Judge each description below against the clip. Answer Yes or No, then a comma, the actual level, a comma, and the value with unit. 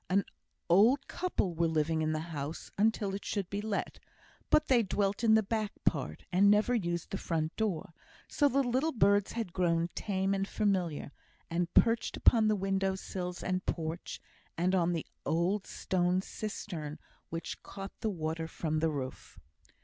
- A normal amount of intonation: Yes, average, 3.9 semitones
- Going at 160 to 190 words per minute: Yes, average, 170 wpm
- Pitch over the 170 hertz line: Yes, high, 190 Hz